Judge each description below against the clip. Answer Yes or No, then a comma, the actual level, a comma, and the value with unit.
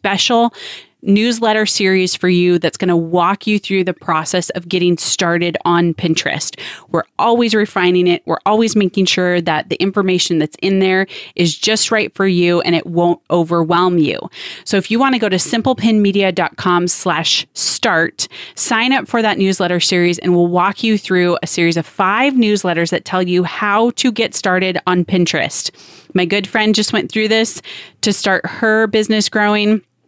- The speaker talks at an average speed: Yes, average, 175 wpm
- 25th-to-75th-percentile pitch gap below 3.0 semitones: No, average, 3.4 semitones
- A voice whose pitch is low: No, medium, 185 Hz